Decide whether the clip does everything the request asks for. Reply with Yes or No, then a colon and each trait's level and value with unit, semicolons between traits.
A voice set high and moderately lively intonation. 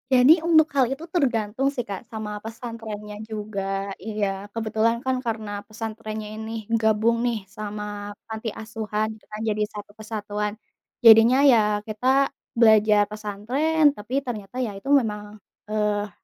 No: high, 220 Hz; narrow, 1.7 semitones